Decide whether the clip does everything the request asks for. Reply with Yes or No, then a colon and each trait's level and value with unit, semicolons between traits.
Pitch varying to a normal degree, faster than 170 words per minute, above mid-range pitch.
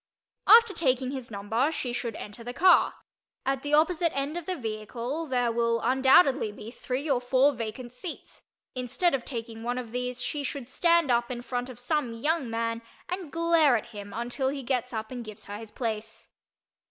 Yes: average, 3.6 semitones; average, 190 wpm; very high, 250 Hz